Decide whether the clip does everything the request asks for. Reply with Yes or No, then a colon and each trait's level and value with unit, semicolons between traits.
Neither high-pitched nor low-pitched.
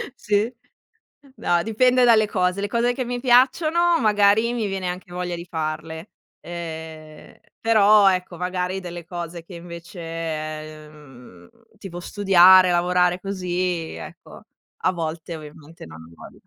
Yes: medium, 180 Hz